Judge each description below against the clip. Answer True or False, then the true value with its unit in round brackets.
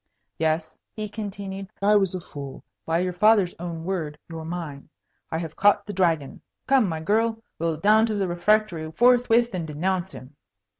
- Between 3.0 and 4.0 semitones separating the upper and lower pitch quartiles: False (4.5 semitones)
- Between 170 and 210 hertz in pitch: True (185 Hz)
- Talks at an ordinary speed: True (170 wpm)